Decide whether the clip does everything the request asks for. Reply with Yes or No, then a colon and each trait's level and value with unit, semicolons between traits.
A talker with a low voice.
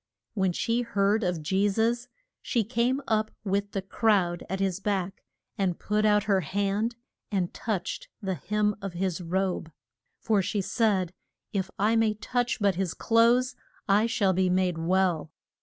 No: high, 200 Hz